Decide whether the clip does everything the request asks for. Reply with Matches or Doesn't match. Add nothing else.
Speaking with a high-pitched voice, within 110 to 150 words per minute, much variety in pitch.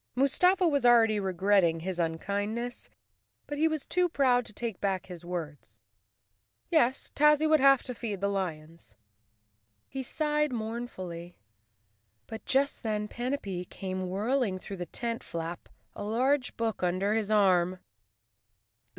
Matches